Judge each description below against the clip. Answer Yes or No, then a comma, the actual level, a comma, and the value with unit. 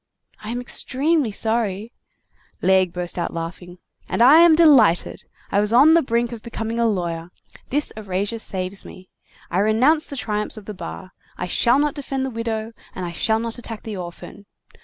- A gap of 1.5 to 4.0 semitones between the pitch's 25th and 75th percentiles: No, average, 4.7 semitones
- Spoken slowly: No, average, 180 wpm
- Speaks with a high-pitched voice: Yes, high, 220 Hz